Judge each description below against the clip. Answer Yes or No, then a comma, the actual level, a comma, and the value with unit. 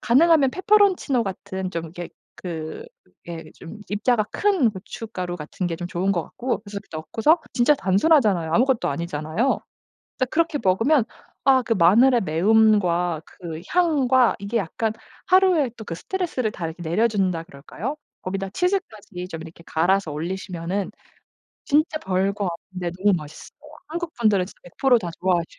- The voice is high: Yes, high, 200 Hz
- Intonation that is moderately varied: No, wide, 6.9 semitones